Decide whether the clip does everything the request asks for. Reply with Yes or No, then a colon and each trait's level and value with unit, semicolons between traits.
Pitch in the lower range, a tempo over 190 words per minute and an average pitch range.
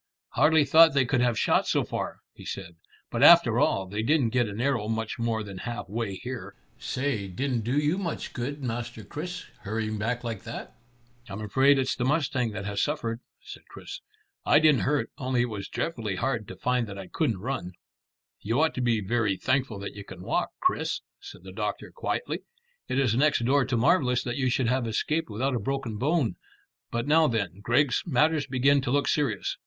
Yes: low, 125 Hz; average, 200 wpm; average, 4.3 semitones